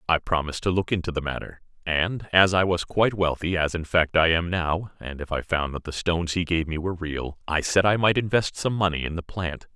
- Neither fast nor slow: No, fast, 250 wpm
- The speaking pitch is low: Yes, very low, 85 Hz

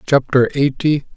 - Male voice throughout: Yes, male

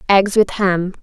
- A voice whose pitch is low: No, high, 190 Hz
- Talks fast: No, average, 175 wpm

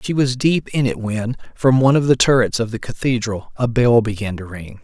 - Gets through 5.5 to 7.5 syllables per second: No, 5.3 syllables/s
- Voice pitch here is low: Yes, low, 120 Hz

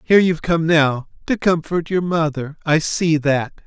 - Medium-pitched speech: Yes, medium, 160 Hz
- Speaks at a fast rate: No, average, 180 wpm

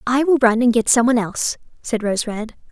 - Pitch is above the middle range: Yes, high, 235 Hz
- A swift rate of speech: Yes, fast, 220 wpm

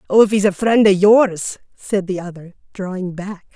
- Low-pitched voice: No, high, 195 Hz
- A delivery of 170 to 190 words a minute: No, fast, 205 wpm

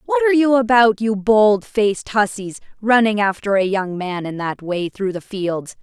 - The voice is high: Yes, high, 210 Hz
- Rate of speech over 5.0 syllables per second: No, 4.6 syllables/s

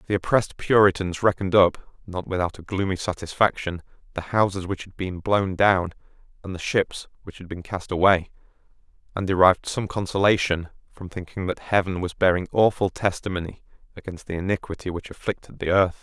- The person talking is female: No, male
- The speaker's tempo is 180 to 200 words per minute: No, average, 165 wpm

